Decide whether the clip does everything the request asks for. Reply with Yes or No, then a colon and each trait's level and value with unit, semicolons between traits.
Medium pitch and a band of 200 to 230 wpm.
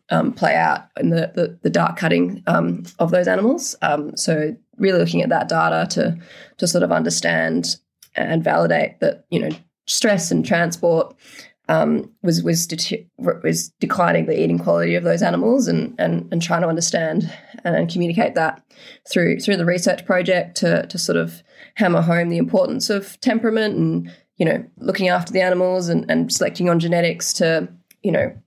No: medium, 170 Hz; average, 175 wpm